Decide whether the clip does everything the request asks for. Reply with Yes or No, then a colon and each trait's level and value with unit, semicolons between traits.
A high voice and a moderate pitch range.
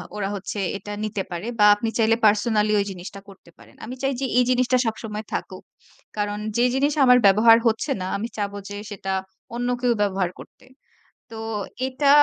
Yes: high, 215 Hz; average, 3.2 semitones